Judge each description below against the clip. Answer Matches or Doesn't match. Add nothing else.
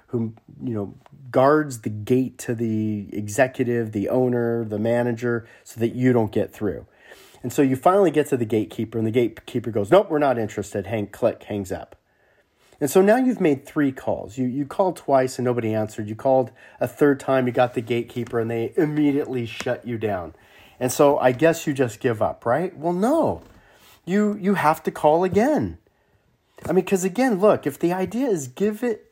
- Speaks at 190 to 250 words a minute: Matches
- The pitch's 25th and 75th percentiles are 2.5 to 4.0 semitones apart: Doesn't match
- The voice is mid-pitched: Doesn't match